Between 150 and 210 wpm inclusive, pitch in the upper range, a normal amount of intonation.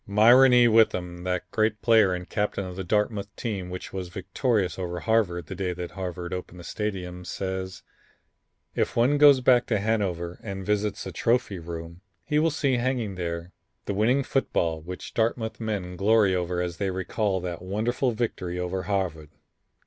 No: average, 170 wpm; very low, 95 Hz; average, 3.9 semitones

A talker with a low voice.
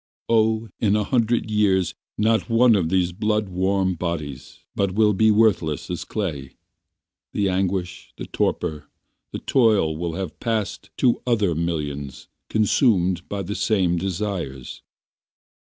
Yes: very low, 95 Hz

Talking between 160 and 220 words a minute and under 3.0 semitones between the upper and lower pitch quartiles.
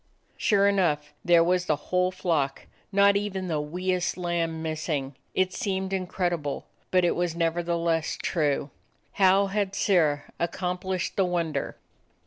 No: average, 140 wpm; narrow, 2.6 semitones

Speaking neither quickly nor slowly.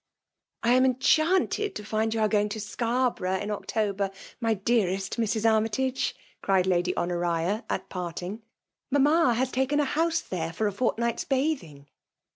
Yes: average, 165 wpm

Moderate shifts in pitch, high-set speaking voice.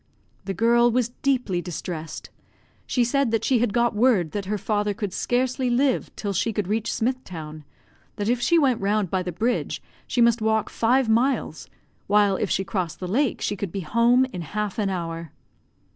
Yes: average, 4.2 semitones; high, 215 Hz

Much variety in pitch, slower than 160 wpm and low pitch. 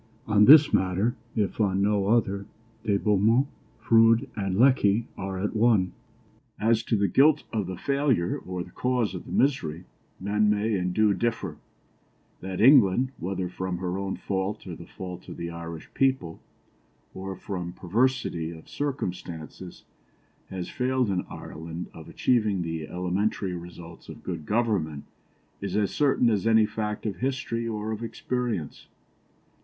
No: average, 4.2 semitones; average, 150 wpm; low, 100 Hz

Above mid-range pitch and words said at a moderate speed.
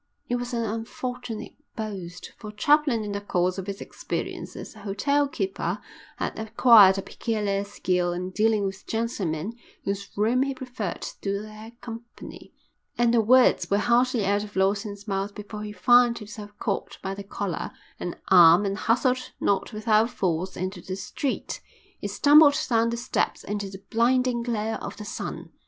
Yes: high, 210 Hz; average, 170 wpm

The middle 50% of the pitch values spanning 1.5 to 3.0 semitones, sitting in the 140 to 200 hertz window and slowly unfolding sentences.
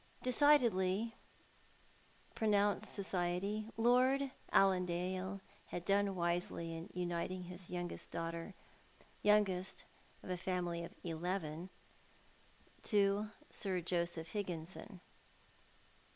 Yes: average, 2.7 semitones; medium, 185 Hz; slow, 90 wpm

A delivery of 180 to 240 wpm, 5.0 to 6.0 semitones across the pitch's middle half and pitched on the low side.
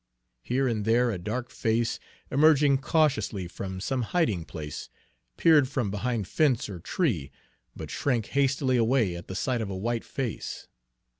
No: average, 155 wpm; wide, 5.4 semitones; low, 120 Hz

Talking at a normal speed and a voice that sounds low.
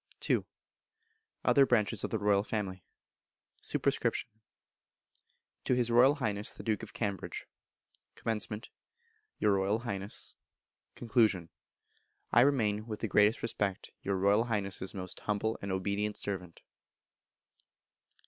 No: slow, 115 wpm; low, 105 Hz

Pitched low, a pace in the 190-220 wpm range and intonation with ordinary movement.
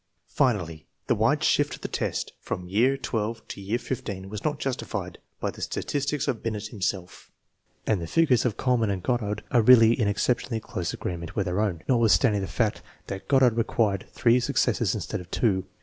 Yes: low, 110 Hz; average, 195 wpm; average, 4.2 semitones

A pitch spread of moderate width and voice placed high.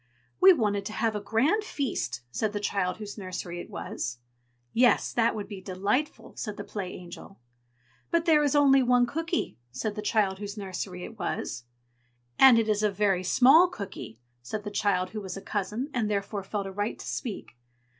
Yes: average, 4.0 semitones; high, 210 Hz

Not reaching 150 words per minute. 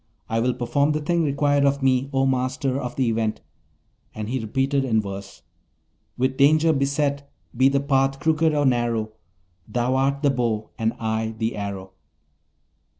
No: average, 160 wpm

